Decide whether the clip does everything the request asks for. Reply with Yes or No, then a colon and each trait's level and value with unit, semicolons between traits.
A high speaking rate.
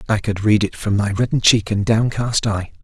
Yes: fast, 235 wpm